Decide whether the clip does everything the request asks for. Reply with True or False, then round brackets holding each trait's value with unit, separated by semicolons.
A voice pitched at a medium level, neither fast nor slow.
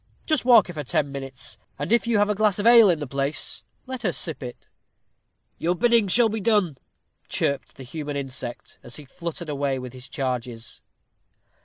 True (155 Hz; 190 wpm)